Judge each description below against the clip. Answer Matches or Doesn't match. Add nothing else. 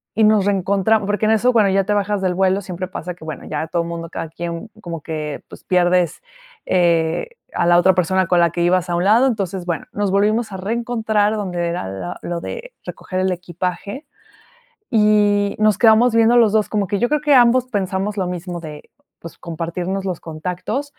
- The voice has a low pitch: Doesn't match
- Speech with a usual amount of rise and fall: Matches